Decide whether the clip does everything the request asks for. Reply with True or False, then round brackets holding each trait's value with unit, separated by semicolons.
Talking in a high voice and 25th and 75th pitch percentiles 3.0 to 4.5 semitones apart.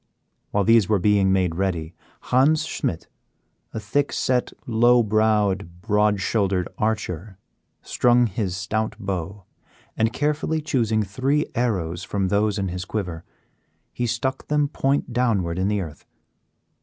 False (105 Hz; 4.2 semitones)